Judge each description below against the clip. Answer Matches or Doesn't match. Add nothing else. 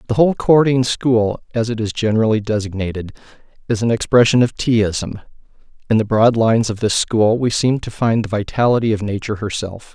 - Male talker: Matches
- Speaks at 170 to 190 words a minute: Matches